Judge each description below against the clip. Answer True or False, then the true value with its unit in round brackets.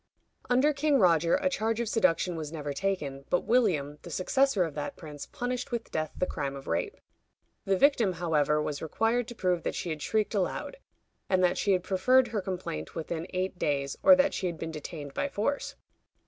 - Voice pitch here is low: False (185 Hz)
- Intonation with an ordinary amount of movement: False (7.1 semitones)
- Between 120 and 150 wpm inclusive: False (200 wpm)